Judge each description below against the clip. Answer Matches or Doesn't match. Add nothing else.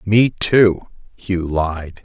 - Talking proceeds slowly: Matches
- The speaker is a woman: Doesn't match